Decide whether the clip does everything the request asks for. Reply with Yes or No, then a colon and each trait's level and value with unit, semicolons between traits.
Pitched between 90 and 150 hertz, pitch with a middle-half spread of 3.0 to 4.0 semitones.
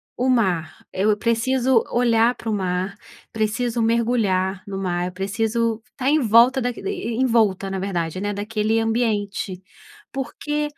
No: high, 225 Hz; average, 3.7 semitones